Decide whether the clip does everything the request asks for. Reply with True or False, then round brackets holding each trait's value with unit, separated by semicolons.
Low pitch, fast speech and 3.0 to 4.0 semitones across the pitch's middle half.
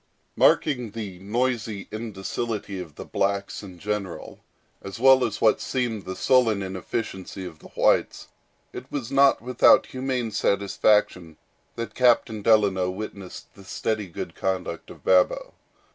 False (105 Hz; 135 wpm; 3.7 semitones)